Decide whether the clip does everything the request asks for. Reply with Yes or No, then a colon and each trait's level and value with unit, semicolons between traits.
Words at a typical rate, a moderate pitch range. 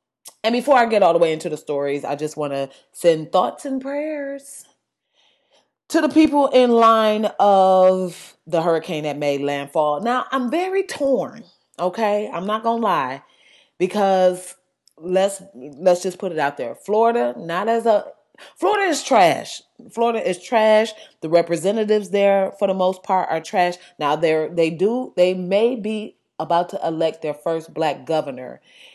No: average, 165 wpm; wide, 5.7 semitones